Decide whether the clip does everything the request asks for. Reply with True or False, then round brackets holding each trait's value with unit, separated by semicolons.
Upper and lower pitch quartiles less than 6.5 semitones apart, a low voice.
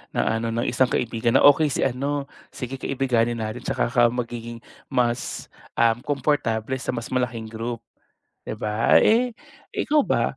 True (2.5 semitones; 120 Hz)